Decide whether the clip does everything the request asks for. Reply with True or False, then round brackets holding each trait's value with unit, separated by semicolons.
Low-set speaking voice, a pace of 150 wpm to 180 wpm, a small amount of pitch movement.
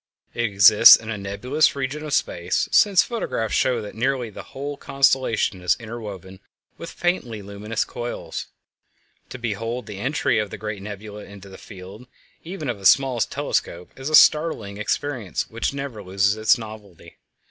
False (110 Hz; 160 wpm; 4.8 semitones)